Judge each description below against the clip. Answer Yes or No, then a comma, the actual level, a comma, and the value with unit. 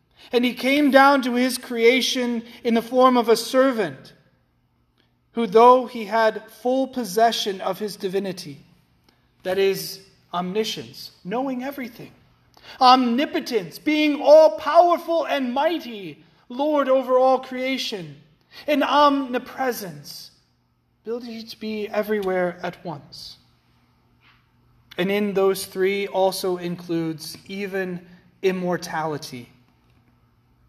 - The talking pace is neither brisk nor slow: No, slow, 105 wpm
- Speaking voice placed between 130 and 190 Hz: No, high, 215 Hz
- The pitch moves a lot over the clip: Yes, wide, 6.3 semitones